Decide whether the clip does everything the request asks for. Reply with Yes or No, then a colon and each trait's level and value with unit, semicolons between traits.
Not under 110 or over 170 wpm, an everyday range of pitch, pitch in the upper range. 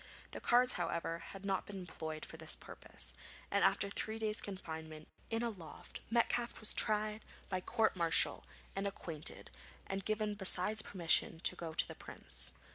Yes: average, 165 wpm; average, 4.5 semitones; high, 195 Hz